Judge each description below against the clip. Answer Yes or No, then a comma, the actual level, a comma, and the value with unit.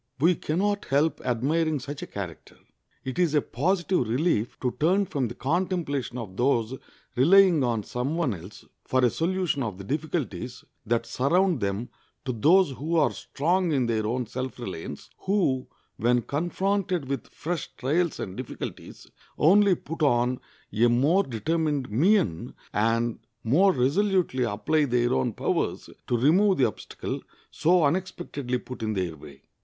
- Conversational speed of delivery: Yes, average, 155 wpm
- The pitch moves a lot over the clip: Yes, wide, 6.3 semitones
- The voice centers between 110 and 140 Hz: Yes, low, 135 Hz